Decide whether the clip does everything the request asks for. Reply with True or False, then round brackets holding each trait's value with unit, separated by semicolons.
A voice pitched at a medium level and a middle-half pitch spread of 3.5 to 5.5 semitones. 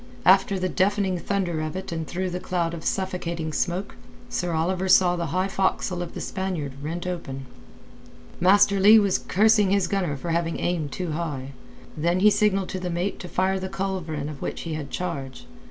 False (180 Hz; 2.5 semitones)